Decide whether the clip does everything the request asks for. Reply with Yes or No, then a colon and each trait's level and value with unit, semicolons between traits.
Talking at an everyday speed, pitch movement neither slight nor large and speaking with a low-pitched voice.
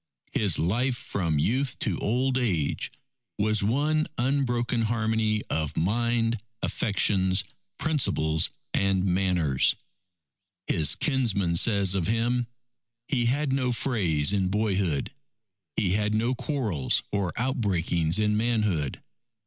No: slow, 110 wpm; average, 4.7 semitones; low, 105 Hz